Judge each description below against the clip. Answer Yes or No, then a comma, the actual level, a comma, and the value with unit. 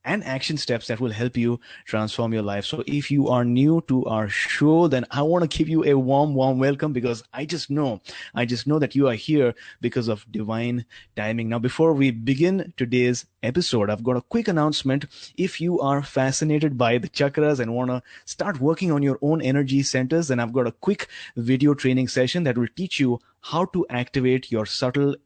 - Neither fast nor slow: No, fast, 210 wpm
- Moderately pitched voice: No, low, 130 Hz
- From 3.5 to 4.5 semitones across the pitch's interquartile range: Yes, average, 3.8 semitones